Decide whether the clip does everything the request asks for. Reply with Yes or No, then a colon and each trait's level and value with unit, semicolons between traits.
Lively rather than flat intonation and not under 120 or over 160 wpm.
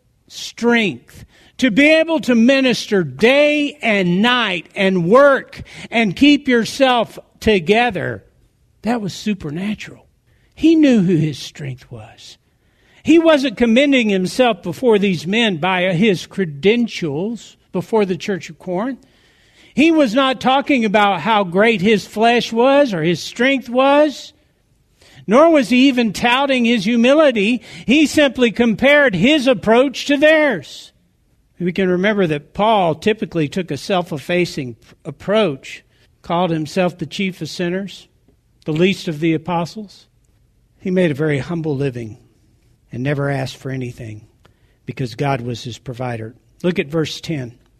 Yes: wide, 7.6 semitones; slow, 135 wpm